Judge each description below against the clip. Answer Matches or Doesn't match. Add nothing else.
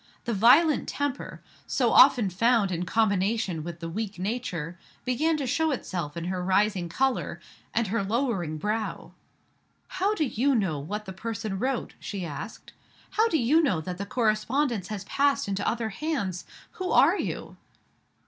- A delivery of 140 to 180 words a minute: Matches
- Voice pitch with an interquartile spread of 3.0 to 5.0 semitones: Doesn't match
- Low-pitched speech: Doesn't match